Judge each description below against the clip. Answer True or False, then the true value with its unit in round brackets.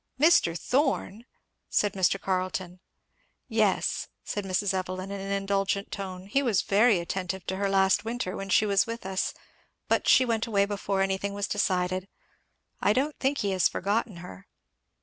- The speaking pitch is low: False (195 Hz)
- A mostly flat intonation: True (2.2 semitones)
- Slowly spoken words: False (165 wpm)